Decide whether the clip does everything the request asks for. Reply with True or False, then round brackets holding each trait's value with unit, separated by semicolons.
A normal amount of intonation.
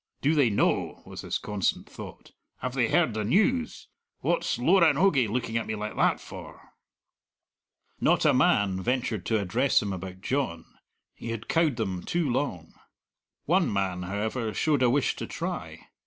False (6.0 semitones)